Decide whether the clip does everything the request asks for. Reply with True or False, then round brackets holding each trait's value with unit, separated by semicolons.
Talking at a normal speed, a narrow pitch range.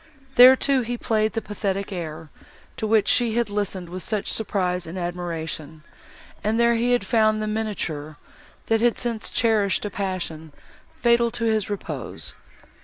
False (155 wpm; 4.1 semitones)